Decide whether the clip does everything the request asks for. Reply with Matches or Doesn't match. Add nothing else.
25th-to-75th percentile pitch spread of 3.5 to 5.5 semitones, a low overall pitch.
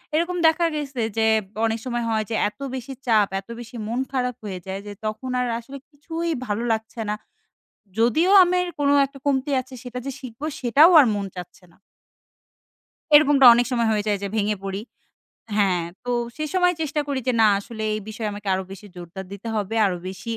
Doesn't match